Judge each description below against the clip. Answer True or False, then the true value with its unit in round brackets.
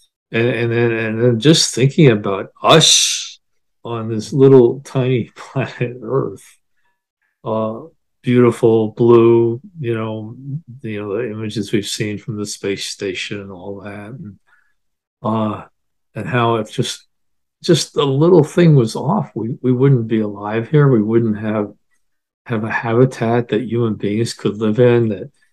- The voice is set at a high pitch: False (115 Hz)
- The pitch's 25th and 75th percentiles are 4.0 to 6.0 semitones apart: False (2.9 semitones)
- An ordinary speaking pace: True (150 wpm)